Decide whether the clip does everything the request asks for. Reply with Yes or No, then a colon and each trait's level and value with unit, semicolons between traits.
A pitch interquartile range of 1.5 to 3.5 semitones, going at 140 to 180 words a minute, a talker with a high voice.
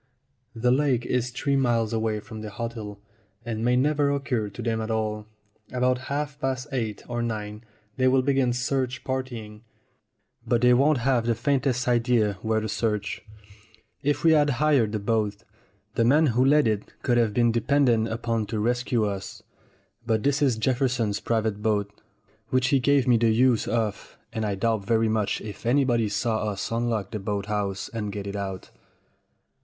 No: average, 3.1 semitones; average, 175 wpm; low, 115 Hz